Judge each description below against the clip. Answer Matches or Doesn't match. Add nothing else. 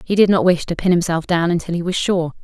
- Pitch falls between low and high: Matches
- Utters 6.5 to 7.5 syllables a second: Doesn't match